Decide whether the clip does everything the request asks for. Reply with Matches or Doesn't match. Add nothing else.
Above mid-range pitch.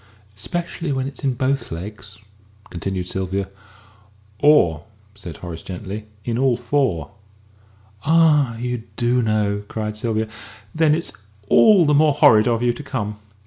Doesn't match